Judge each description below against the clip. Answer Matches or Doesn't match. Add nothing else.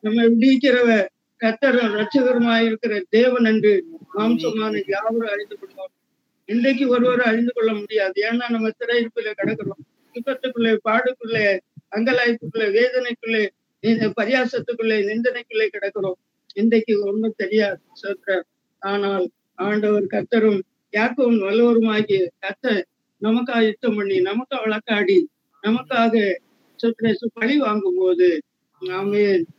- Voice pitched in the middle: Doesn't match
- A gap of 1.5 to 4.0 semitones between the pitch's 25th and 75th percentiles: Matches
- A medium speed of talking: Matches